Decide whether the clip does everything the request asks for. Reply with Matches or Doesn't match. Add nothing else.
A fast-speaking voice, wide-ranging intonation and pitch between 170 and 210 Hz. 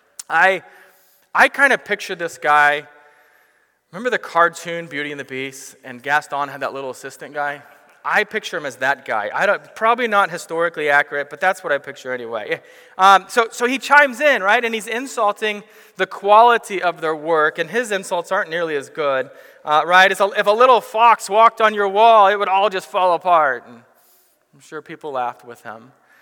Doesn't match